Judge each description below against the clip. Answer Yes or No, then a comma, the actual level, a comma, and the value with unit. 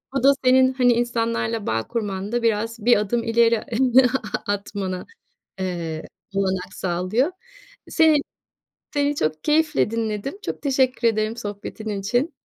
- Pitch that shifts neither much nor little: Yes, average, 4.1 semitones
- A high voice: Yes, high, 230 Hz